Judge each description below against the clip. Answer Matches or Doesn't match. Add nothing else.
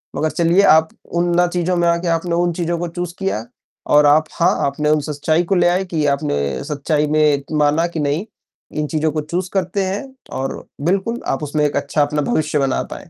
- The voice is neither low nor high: Matches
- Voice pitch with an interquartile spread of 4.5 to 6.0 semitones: Doesn't match